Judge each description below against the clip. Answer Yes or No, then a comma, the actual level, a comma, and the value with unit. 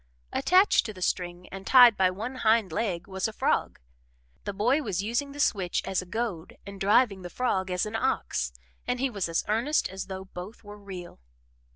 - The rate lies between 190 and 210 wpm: Yes, average, 200 wpm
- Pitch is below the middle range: No, high, 200 Hz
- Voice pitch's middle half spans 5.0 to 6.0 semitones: No, average, 4.0 semitones